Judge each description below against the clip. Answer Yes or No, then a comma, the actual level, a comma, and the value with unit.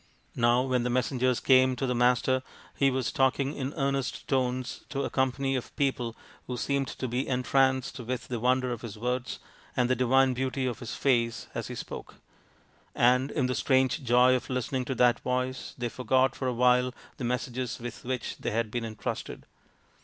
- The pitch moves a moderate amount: No, narrow, 1.2 semitones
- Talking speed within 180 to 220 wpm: Yes, average, 190 wpm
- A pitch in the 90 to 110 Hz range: No, low, 125 Hz